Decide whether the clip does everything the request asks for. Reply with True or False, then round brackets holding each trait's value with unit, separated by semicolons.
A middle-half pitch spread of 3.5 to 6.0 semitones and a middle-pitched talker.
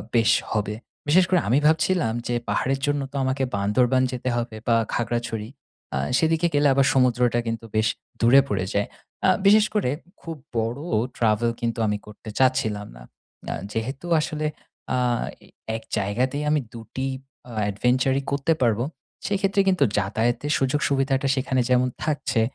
False (4.1 semitones; 125 Hz)